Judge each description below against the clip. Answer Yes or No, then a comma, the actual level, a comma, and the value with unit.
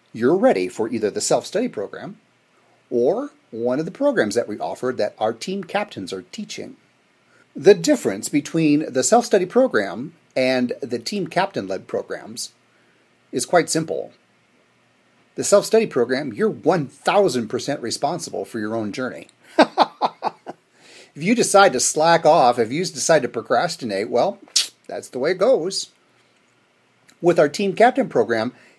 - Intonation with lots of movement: Yes, wide, 8.3 semitones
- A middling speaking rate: Yes, average, 150 wpm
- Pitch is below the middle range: No, medium, 180 Hz